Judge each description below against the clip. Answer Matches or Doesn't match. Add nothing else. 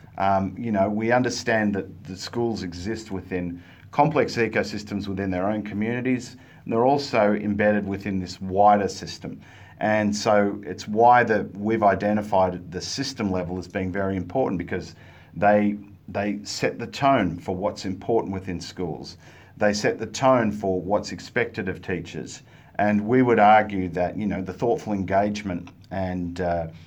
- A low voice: Matches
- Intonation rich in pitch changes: Doesn't match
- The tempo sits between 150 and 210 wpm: Matches